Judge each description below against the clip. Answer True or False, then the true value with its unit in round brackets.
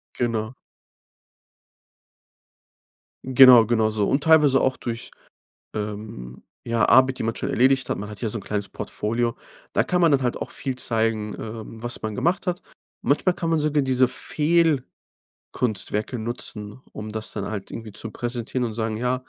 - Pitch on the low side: True (120 Hz)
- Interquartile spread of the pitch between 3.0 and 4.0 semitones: True (3.4 semitones)